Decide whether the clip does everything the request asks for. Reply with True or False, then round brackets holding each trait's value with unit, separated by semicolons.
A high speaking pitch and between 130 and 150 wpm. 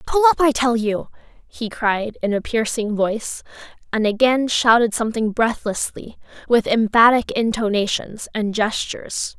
True (230 Hz; 135 wpm)